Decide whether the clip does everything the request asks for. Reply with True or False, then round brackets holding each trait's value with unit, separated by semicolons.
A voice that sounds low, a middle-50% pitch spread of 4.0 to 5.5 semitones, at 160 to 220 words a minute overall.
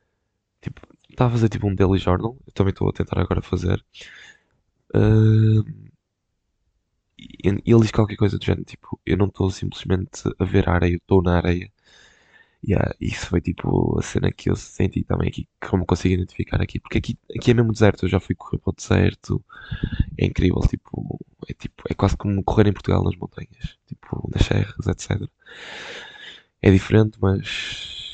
False (100 Hz; 3.2 semitones; 180 wpm)